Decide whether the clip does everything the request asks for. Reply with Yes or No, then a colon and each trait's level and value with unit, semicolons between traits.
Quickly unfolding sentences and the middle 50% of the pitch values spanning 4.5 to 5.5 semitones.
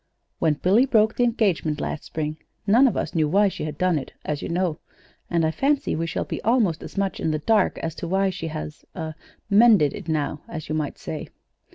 Yes: fast, 225 wpm; average, 5.1 semitones